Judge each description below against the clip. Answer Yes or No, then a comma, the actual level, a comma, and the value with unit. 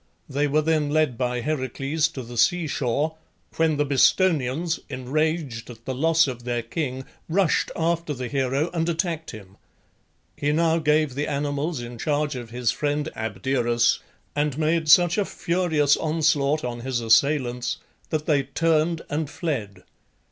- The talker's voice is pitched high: No, medium, 145 Hz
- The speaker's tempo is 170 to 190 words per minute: No, average, 155 wpm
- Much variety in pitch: No, average, 4.1 semitones